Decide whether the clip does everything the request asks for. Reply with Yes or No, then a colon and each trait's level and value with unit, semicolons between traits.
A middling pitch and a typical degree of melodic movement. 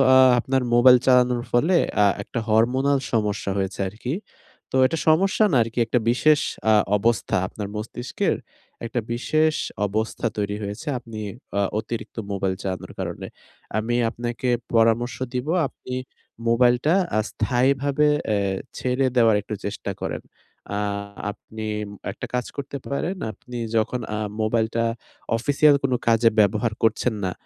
No: low, 120 Hz; average, 3.2 semitones